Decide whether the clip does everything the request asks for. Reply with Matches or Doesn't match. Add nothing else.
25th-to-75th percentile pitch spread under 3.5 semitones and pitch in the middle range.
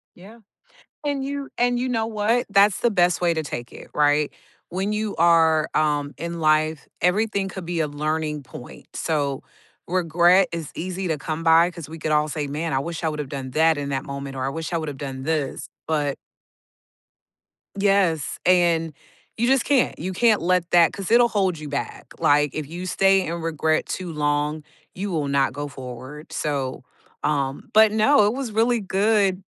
Doesn't match